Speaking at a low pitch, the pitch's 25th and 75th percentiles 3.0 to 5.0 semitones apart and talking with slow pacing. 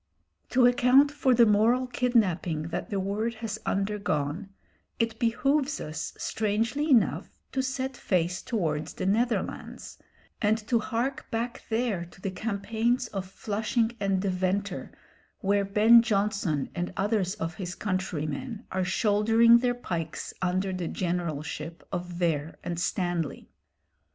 No: high, 205 Hz; average, 4.5 semitones; slow, 130 wpm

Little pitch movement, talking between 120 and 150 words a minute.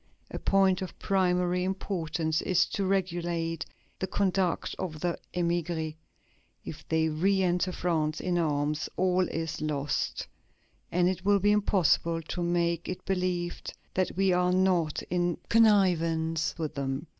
Yes: narrow, 2.3 semitones; average, 140 wpm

